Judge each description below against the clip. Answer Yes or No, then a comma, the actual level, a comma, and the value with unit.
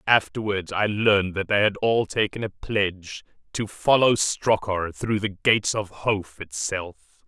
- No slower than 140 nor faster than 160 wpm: Yes, average, 155 wpm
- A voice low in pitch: Yes, low, 100 Hz